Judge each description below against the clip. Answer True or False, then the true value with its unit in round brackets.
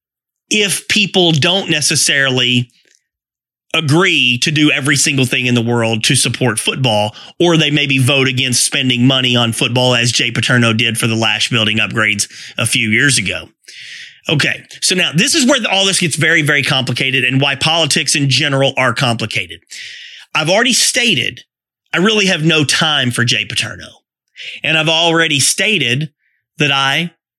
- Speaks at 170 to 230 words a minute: False (160 wpm)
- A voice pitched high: False (135 Hz)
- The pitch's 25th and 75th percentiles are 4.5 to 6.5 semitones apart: True (5.0 semitones)